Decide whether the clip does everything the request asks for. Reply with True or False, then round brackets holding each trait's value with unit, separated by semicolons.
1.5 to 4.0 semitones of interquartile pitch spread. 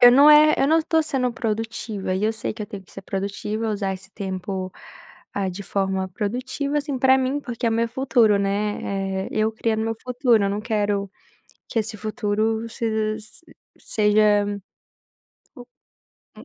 True (3.3 semitones)